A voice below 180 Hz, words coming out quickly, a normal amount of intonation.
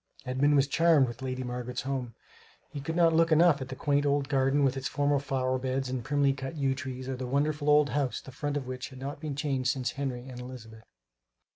No: low, 135 Hz; fast, 230 wpm; narrow, 2.0 semitones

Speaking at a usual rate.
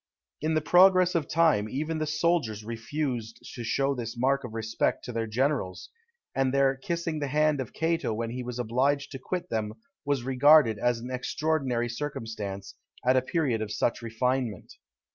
Yes: average, 175 wpm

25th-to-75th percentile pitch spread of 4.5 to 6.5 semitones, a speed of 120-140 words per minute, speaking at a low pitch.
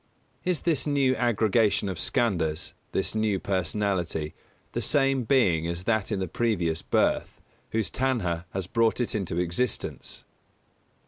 Yes: wide, 5.5 semitones; slow, 135 wpm; low, 105 Hz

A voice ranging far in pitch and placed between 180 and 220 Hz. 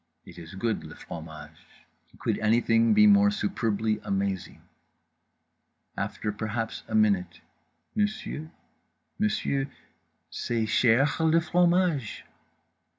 No: wide, 7.3 semitones; low, 115 Hz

